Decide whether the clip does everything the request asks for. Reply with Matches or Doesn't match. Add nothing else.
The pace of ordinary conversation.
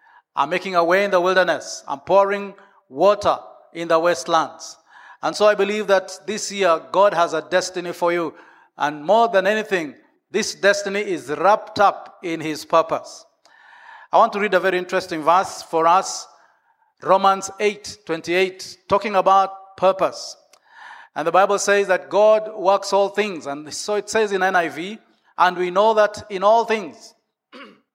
Matches